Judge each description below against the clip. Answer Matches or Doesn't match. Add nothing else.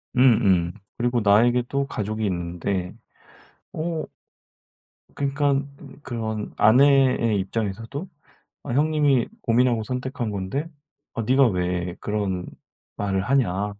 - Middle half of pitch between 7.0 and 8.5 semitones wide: Doesn't match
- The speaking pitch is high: Doesn't match